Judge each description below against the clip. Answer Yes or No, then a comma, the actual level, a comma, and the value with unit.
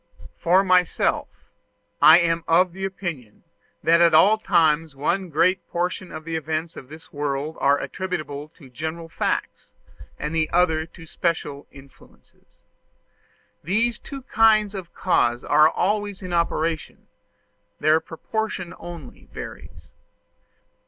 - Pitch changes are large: No, average, 3.0 semitones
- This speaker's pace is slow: Yes, slow, 120 wpm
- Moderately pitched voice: Yes, medium, 165 Hz